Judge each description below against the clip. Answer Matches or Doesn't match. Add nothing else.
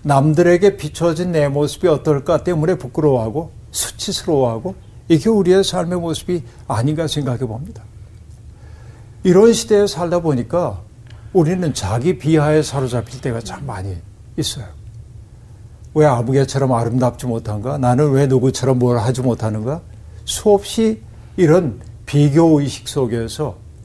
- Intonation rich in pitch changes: Matches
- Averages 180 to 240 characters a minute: Doesn't match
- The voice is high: Doesn't match